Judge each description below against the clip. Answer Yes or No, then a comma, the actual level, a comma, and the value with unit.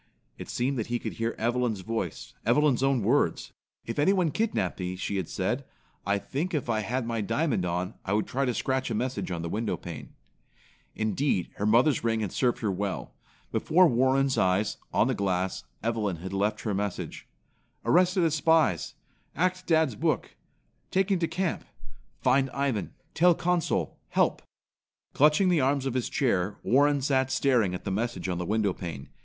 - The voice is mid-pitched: No, low, 120 Hz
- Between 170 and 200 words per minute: Yes, average, 175 wpm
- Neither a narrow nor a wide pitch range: No, wide, 6.2 semitones